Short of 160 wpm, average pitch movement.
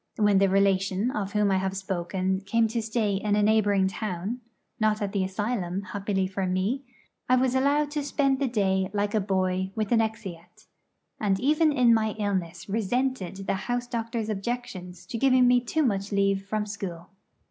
No: average, 180 wpm; average, 3.6 semitones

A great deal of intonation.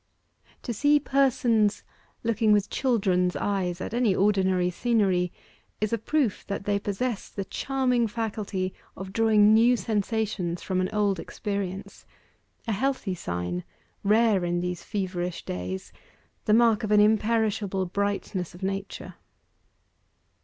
No: average, 3.2 semitones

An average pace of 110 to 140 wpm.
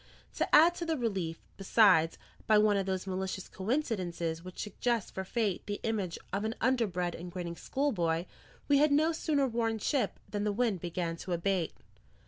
No: average, 175 wpm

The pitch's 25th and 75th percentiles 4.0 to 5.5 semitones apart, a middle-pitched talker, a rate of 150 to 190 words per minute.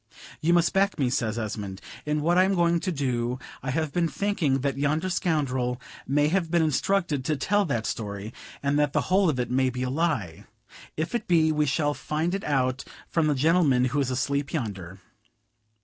No: average, 4.8 semitones; medium, 145 Hz; average, 200 wpm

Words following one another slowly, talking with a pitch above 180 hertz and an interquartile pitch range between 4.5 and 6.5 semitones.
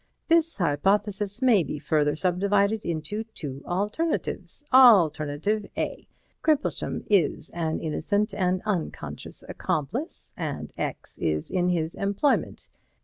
Yes: slow, 110 wpm; high, 190 Hz; average, 5.1 semitones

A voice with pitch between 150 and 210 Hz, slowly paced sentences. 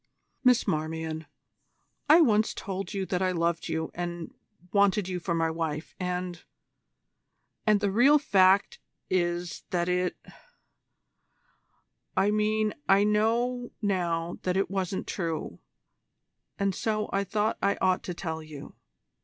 Yes: medium, 185 Hz; slow, 130 wpm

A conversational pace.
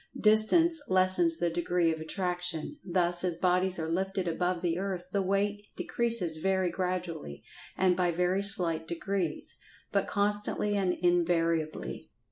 No: slow, 130 wpm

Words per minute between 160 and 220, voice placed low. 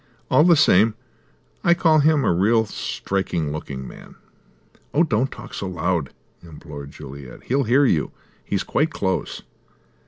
No: average, 145 wpm; low, 100 Hz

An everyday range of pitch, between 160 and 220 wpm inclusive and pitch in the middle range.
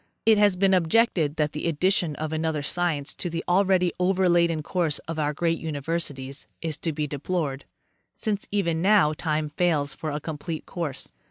Yes: average, 3.1 semitones; average, 170 wpm; medium, 165 Hz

